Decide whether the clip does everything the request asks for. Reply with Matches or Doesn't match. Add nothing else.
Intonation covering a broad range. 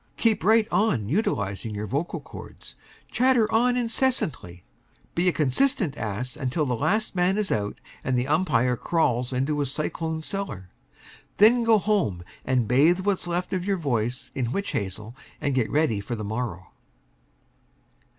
Matches